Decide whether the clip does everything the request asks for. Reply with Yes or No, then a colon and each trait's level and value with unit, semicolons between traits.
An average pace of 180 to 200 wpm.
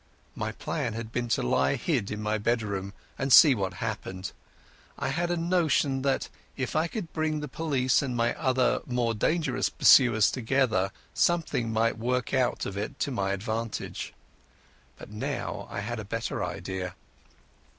No: average, 160 wpm